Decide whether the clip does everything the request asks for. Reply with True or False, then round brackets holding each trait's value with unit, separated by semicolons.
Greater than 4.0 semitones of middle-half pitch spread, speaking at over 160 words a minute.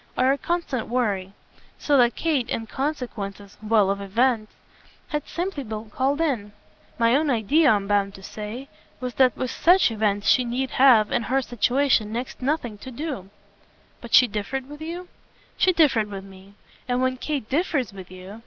True (4.7 semitones; 180 wpm)